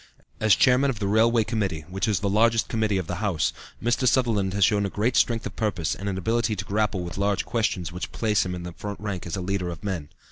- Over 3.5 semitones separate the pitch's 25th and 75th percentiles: No, average, 3.2 semitones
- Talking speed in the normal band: No, fast, 245 wpm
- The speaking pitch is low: Yes, low, 100 Hz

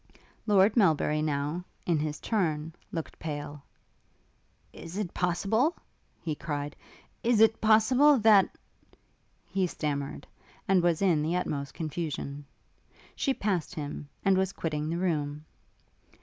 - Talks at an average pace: No, slow, 130 wpm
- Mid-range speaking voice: Yes, medium, 170 Hz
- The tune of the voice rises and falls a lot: No, average, 4.7 semitones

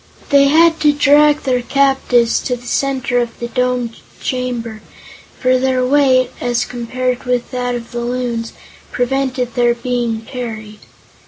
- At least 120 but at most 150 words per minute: Yes, average, 145 wpm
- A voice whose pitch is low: No, very high, 250 Hz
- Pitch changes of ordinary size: No, narrow, 1.8 semitones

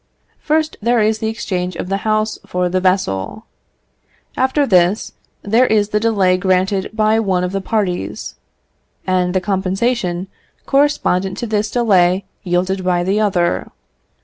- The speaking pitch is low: No, high, 195 Hz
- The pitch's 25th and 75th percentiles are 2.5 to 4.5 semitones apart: Yes, average, 3.1 semitones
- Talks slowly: No, average, 145 wpm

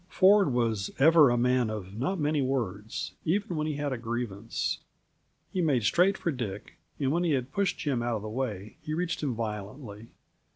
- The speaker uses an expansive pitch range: Yes, wide, 5.8 semitones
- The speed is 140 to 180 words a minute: No, average, 195 wpm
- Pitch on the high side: No, low, 130 Hz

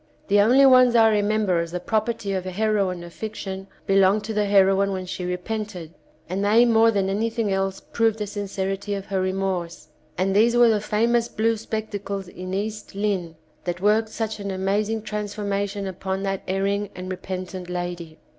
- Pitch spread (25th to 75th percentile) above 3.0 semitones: No, narrow, 2.4 semitones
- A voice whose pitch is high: Yes, high, 200 Hz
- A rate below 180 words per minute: No, average, 185 wpm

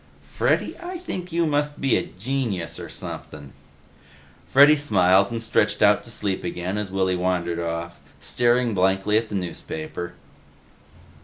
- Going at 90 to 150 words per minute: Yes, average, 145 wpm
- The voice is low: Yes, low, 100 Hz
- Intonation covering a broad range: Yes, wide, 6.0 semitones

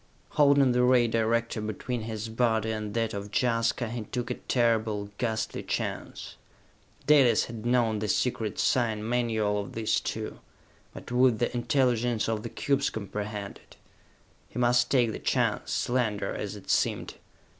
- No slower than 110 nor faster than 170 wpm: Yes, average, 155 wpm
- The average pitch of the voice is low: Yes, low, 115 Hz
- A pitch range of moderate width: No, narrow, 2.2 semitones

